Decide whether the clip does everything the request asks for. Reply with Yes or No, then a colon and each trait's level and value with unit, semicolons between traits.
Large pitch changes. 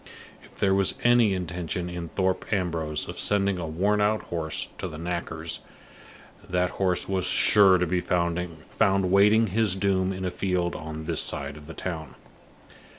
No: narrow, 2.6 semitones